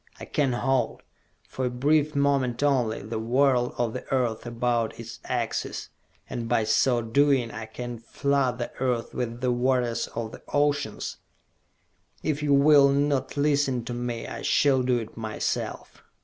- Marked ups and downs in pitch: No, average, 3.0 semitones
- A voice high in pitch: No, low, 125 Hz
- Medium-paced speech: Yes, average, 160 wpm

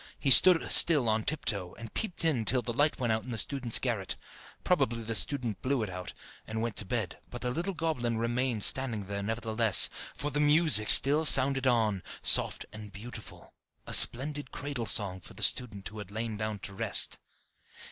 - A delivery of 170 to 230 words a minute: Yes, average, 190 wpm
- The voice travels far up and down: No, average, 4.1 semitones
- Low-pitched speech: Yes, low, 115 Hz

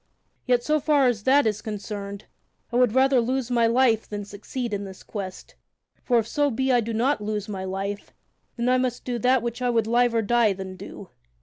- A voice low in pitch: No, high, 230 Hz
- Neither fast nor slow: No, fast, 210 wpm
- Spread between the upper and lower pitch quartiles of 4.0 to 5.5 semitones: No, average, 3.4 semitones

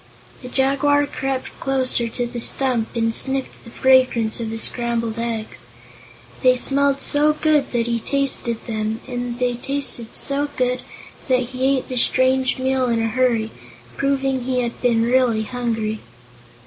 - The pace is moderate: Yes, average, 155 wpm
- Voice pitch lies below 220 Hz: No, very high, 250 Hz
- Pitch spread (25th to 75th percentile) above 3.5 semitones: No, narrow, 2.4 semitones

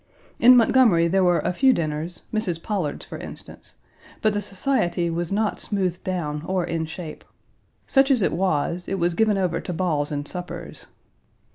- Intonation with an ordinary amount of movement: Yes, average, 3.7 semitones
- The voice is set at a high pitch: No, medium, 180 Hz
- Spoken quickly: No, average, 170 wpm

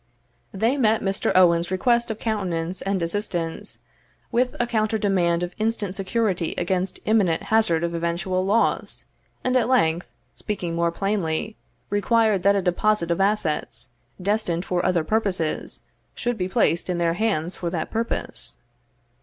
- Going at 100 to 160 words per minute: Yes, average, 145 wpm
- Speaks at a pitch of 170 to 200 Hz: Yes, high, 190 Hz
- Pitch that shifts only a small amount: No, average, 4.2 semitones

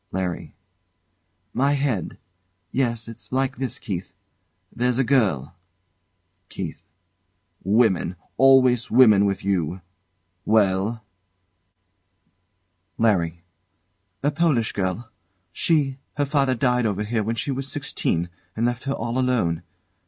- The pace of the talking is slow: Yes, slow, 110 wpm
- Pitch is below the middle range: Yes, low, 115 Hz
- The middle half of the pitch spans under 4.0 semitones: No, average, 5.2 semitones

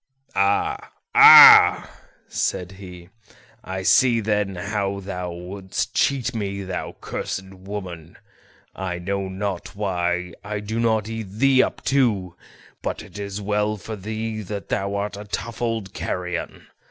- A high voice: No, low, 100 Hz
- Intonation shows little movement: Yes, narrow, 2.3 semitones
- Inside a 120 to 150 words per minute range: Yes, average, 140 wpm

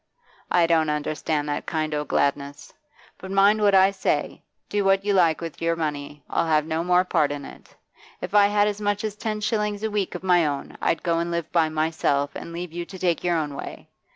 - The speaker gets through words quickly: Yes, fast, 225 wpm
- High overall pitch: No, medium, 170 Hz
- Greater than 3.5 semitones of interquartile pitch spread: Yes, average, 4.2 semitones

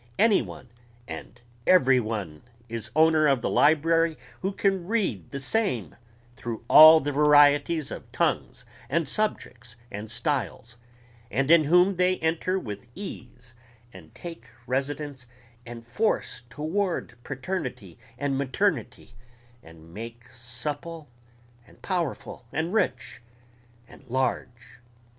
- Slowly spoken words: Yes, slow, 120 wpm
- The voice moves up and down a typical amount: No, wide, 5.8 semitones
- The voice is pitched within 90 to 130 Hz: No, medium, 140 Hz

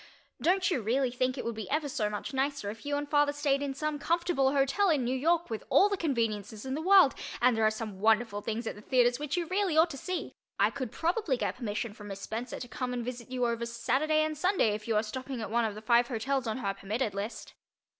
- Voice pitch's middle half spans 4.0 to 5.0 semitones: Yes, average, 4.7 semitones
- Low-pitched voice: No, very high, 255 Hz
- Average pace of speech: No, fast, 255 wpm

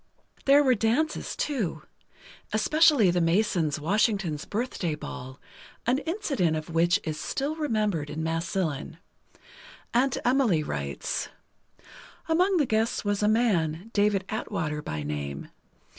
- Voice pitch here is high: Yes, high, 200 Hz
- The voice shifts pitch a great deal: Yes, wide, 7.6 semitones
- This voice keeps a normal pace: No, slow, 120 wpm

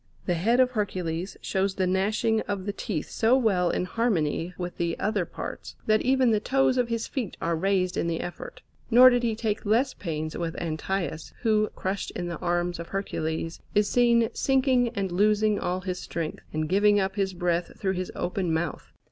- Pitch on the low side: No, high, 195 Hz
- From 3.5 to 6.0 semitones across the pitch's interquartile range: Yes, average, 4.2 semitones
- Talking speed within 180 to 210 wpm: Yes, average, 195 wpm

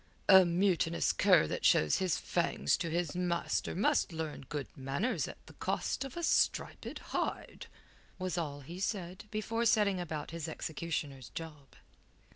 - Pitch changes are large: No, average, 3.8 semitones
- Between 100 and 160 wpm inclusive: Yes, average, 150 wpm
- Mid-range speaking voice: Yes, medium, 170 Hz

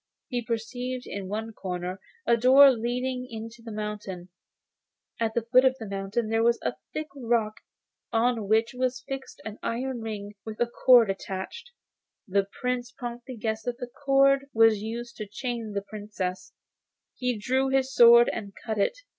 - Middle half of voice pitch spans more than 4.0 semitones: No, average, 2.8 semitones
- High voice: Yes, high, 230 Hz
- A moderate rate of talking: Yes, average, 165 wpm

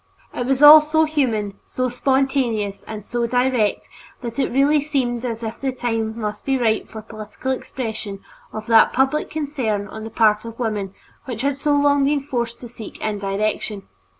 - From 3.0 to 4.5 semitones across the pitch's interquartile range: Yes, average, 3.9 semitones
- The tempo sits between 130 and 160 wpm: No, average, 180 wpm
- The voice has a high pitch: Yes, high, 235 Hz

